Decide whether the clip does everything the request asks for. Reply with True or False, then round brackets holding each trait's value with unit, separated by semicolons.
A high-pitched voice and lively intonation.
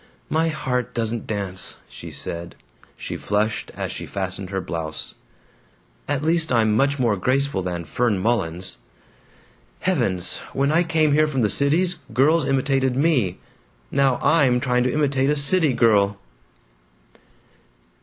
False (125 Hz; 6.0 semitones)